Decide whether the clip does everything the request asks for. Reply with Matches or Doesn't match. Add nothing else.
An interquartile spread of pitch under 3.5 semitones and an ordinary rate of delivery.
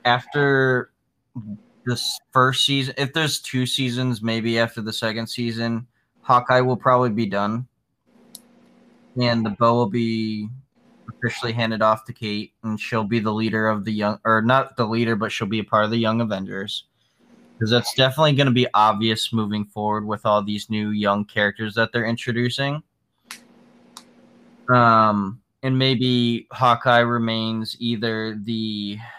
Matches